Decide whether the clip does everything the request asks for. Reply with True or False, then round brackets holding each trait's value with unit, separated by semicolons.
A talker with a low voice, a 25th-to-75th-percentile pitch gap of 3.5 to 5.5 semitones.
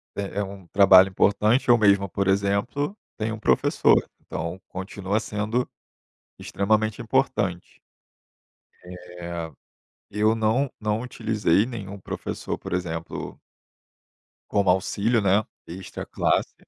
False (100 Hz; 2.5 semitones)